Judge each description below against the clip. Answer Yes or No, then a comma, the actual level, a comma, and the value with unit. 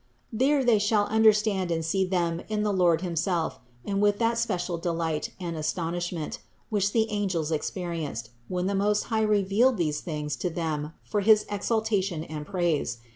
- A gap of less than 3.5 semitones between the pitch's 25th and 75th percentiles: No, average, 4.0 semitones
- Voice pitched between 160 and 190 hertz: Yes, medium, 185 Hz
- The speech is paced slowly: No, average, 170 wpm